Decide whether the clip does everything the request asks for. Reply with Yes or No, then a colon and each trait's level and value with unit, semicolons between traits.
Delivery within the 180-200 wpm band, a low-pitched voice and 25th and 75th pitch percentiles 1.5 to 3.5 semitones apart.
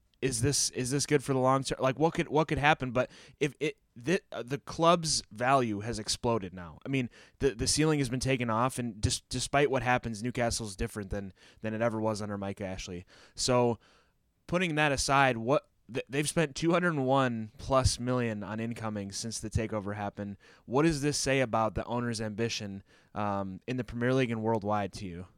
No: average, 195 wpm; low, 120 Hz; average, 4.2 semitones